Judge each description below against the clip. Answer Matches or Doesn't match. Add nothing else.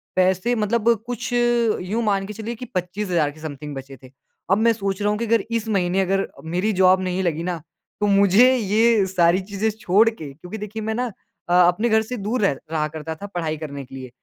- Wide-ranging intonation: Doesn't match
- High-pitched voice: Matches